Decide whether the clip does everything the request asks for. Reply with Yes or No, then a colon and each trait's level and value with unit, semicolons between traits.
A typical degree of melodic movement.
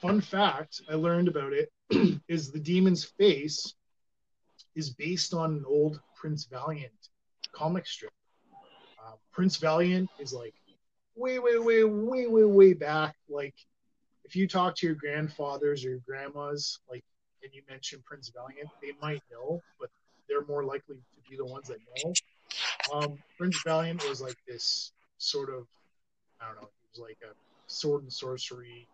No: wide, 6.4 semitones